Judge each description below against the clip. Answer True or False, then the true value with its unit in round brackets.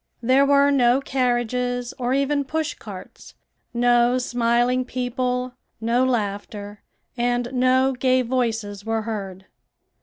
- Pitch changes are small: True (1.8 semitones)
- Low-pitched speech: False (245 Hz)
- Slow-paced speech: True (115 wpm)